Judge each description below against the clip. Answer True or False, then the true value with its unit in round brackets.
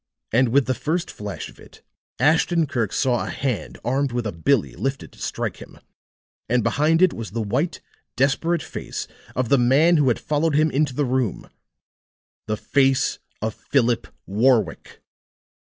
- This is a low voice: True (130 Hz)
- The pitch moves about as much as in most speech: True (3.8 semitones)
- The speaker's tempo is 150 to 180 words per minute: True (165 wpm)